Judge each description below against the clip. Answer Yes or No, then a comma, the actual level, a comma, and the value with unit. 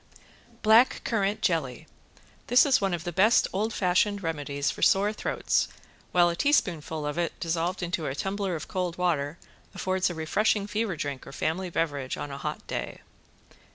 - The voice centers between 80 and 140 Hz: No, medium, 175 Hz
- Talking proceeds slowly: No, average, 170 wpm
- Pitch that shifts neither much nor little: Yes, average, 4.2 semitones